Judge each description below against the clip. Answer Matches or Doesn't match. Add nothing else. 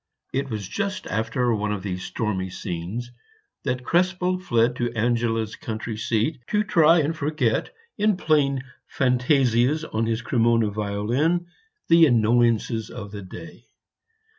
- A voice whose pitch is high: Doesn't match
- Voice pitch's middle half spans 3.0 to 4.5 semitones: Doesn't match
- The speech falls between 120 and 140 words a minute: Matches